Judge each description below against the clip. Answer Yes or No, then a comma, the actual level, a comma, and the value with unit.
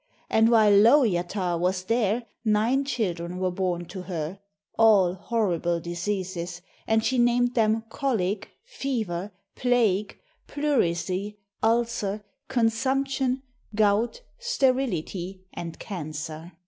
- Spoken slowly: Yes, slow, 100 wpm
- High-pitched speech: Yes, high, 210 Hz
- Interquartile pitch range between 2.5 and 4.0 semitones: No, average, 4.9 semitones